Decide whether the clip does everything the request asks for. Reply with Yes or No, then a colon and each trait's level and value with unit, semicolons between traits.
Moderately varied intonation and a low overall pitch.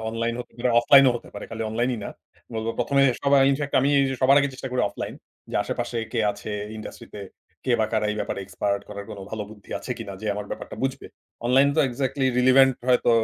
Yes: average, 3.5 semitones; low, 120 Hz